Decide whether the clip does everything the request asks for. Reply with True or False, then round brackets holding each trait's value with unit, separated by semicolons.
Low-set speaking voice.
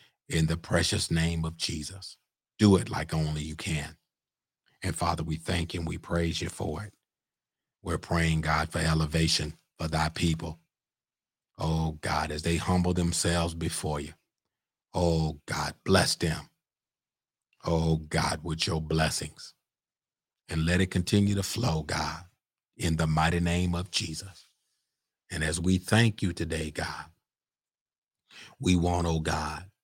True (85 Hz)